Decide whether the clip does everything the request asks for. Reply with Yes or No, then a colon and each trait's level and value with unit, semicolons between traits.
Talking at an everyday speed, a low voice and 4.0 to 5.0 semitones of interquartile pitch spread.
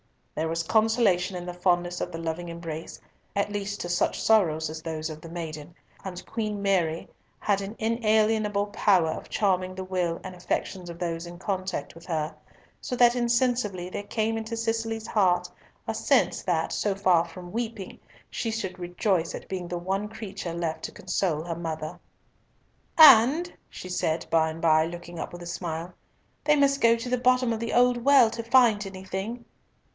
No: average, 180 wpm; high, 190 Hz; average, 4.6 semitones